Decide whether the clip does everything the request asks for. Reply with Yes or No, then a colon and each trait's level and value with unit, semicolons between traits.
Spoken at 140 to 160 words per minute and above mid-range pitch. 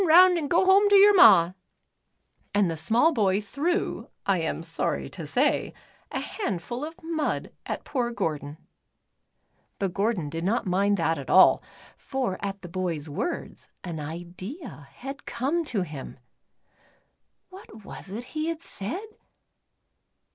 Yes: average, 145 wpm; high, 205 Hz